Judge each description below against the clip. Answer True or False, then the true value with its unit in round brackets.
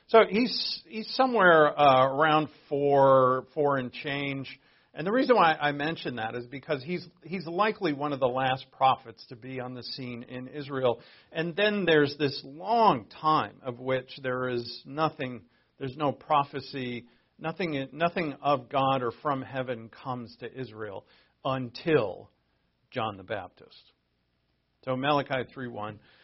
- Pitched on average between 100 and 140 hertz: True (135 Hz)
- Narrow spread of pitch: False (3.6 semitones)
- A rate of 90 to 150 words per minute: True (145 wpm)